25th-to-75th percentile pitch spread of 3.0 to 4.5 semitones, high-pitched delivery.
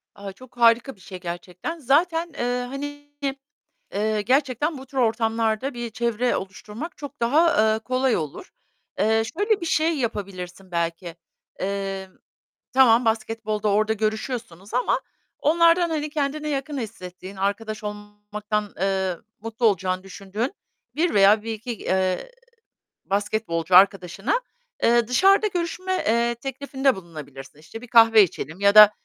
No: average, 5.3 semitones; high, 225 Hz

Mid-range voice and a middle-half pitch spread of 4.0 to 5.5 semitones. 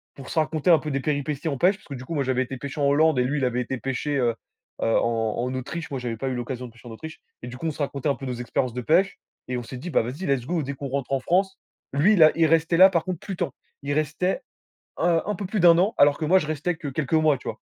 Yes: medium, 145 Hz; average, 4.3 semitones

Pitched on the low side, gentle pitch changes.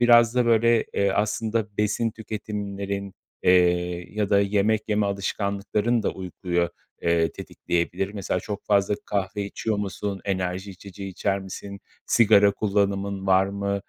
Yes: low, 100 Hz; narrow, 1.7 semitones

